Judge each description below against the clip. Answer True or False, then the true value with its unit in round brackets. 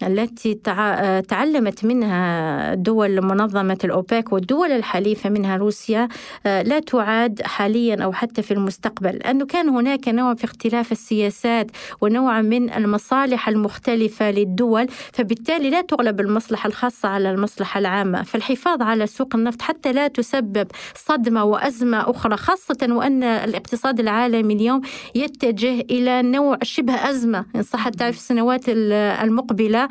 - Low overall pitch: False (230 Hz)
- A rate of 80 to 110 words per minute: False (130 wpm)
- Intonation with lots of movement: False (3.3 semitones)